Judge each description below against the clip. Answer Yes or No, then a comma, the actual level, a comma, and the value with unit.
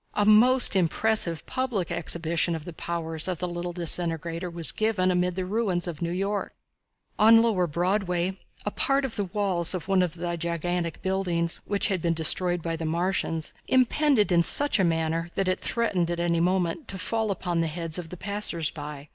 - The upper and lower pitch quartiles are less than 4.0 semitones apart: Yes, average, 3.0 semitones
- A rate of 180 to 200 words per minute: Yes, average, 190 wpm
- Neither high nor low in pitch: Yes, medium, 180 Hz